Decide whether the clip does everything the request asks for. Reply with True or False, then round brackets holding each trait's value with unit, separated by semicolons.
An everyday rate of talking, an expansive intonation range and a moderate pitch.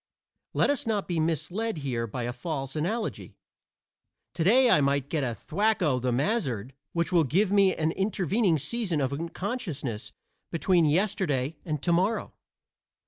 True (150 wpm; 6.2 semitones; 165 Hz)